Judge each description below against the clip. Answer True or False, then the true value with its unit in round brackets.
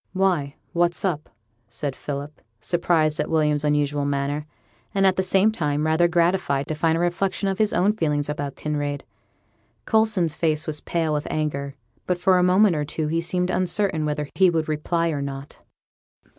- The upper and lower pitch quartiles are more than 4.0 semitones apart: False (3.5 semitones)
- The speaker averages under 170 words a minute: False (175 wpm)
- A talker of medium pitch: True (160 Hz)